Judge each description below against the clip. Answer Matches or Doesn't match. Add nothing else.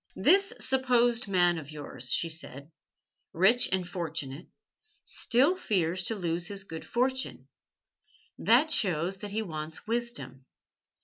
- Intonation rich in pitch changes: Matches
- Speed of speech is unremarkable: Doesn't match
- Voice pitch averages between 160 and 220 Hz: Matches